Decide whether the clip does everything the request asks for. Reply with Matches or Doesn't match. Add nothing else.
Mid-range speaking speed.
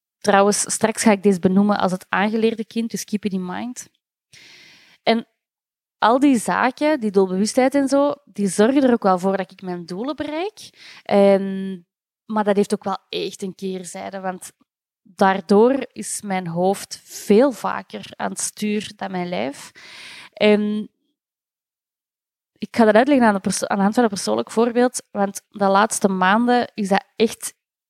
Matches